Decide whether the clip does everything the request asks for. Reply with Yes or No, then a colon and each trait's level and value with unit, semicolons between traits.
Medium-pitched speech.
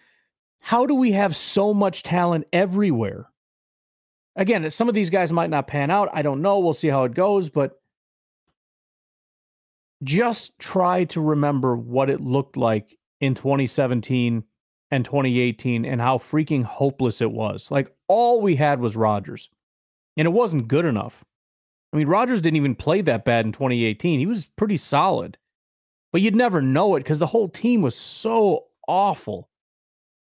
Yes: medium, 145 Hz